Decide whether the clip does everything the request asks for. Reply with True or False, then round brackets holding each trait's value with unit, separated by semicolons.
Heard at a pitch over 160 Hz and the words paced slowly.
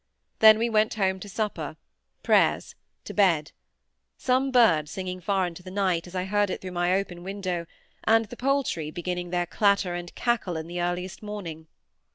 False (185 Hz; 170 wpm)